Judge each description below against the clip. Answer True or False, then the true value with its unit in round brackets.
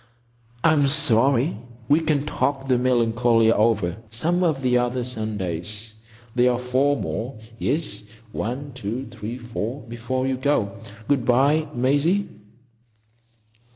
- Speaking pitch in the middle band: False (125 Hz)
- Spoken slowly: True (115 wpm)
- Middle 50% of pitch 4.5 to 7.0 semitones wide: False (3.8 semitones)